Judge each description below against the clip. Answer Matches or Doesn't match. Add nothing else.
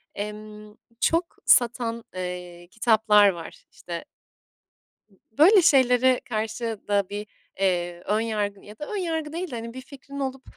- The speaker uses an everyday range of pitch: Matches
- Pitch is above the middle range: Matches